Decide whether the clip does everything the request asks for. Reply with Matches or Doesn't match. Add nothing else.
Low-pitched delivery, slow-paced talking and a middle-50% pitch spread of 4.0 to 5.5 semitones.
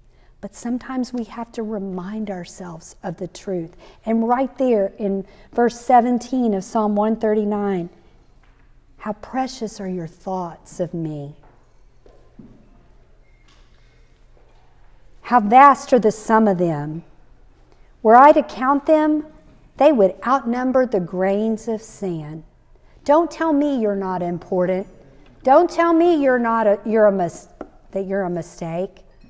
Doesn't match